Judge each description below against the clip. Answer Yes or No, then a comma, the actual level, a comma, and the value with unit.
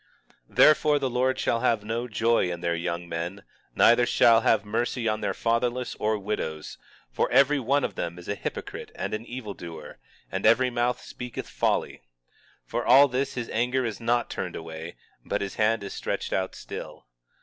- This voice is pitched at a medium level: No, low, 115 Hz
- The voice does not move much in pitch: No, average, 4.4 semitones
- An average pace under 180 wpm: No, average, 185 wpm